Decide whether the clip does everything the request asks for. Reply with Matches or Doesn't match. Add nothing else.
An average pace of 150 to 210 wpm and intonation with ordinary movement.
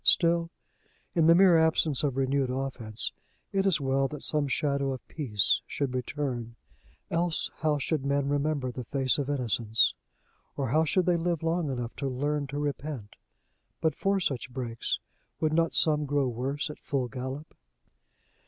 Matches